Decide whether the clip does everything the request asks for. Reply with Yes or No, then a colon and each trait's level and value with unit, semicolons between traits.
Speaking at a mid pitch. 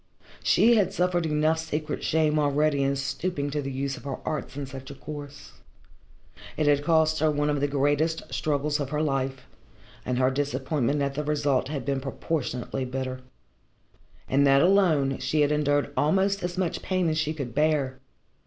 Yes: medium, 145 Hz